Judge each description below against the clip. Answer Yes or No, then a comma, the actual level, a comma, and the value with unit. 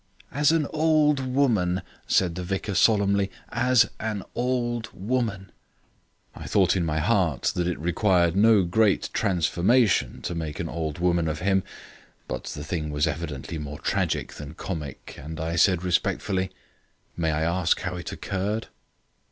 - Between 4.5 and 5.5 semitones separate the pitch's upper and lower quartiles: Yes, average, 5.1 semitones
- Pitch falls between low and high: No, very low, 95 Hz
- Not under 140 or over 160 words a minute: Yes, average, 150 wpm